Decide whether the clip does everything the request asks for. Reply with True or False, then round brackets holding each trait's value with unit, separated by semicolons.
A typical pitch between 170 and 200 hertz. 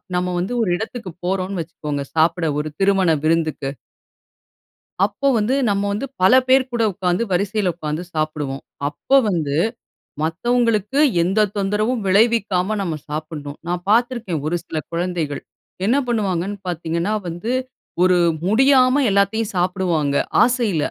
True (185 Hz)